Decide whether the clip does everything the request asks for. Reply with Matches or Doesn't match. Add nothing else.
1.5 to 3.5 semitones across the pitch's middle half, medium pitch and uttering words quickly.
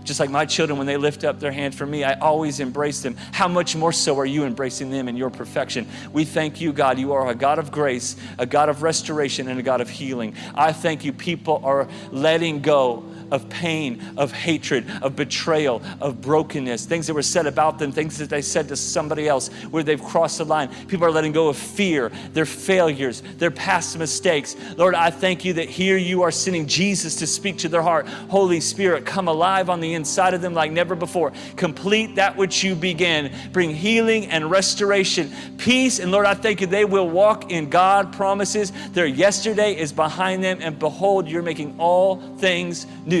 Doesn't match